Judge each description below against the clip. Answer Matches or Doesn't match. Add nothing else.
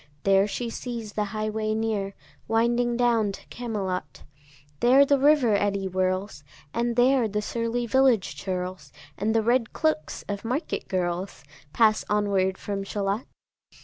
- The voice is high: Matches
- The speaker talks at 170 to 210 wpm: Doesn't match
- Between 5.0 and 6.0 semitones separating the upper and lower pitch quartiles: Doesn't match